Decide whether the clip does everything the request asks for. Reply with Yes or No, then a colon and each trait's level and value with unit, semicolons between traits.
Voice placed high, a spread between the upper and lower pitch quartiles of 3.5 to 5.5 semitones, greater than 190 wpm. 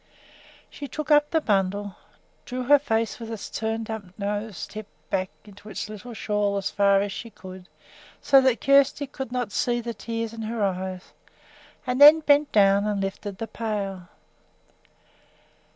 No: high, 220 Hz; average, 3.9 semitones; average, 165 wpm